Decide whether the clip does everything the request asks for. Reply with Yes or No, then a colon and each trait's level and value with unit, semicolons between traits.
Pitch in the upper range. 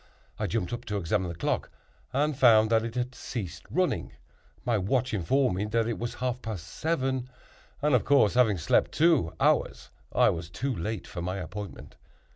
No: low, 115 Hz